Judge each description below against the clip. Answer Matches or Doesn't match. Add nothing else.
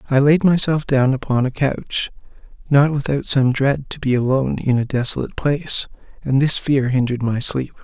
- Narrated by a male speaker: Matches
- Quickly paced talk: Doesn't match